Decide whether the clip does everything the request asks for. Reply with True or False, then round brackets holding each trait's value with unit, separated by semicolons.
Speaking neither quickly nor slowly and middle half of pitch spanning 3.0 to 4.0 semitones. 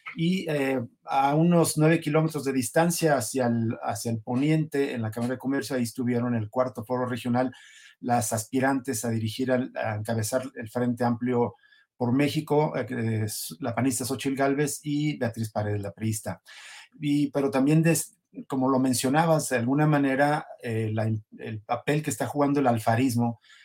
True (165 wpm; 3.4 semitones)